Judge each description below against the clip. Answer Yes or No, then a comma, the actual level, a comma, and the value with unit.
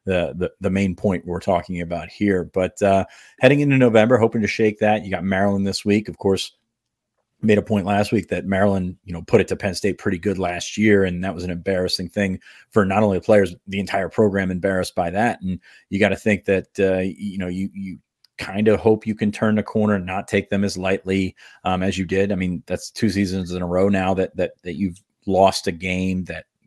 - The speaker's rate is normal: No, fast, 235 wpm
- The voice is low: Yes, very low, 95 Hz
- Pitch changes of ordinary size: No, narrow, 2.1 semitones